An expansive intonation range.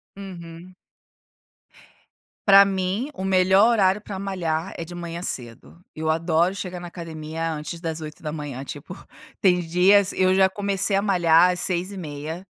No: average, 2.8 semitones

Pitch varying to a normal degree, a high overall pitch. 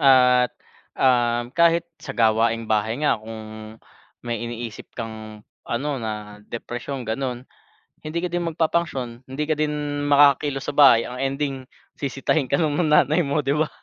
No: average, 4.1 semitones; low, 130 Hz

